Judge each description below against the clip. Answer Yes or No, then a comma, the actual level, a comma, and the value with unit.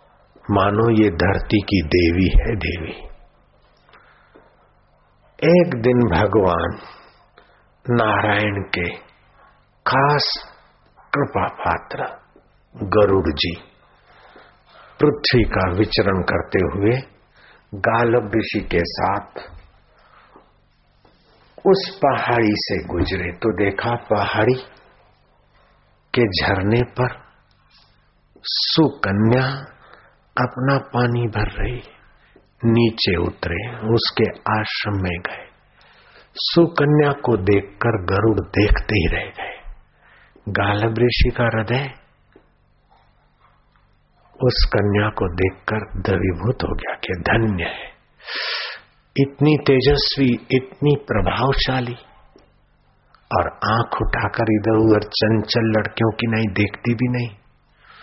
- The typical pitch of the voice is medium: No, low, 110 Hz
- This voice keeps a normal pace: No, slow, 90 wpm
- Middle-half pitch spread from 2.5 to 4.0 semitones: Yes, average, 3.6 semitones